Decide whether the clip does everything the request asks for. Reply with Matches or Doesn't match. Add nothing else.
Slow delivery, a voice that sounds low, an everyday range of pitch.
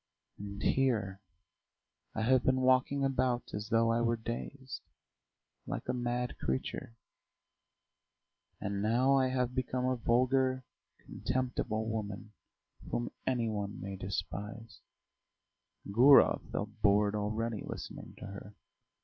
Matches